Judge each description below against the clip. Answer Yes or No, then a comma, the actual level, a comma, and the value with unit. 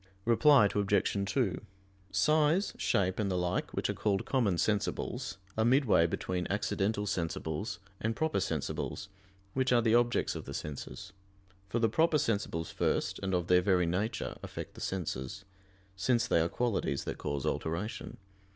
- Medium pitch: No, low, 100 Hz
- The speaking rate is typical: Yes, average, 155 wpm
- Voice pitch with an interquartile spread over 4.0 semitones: Yes, average, 4.7 semitones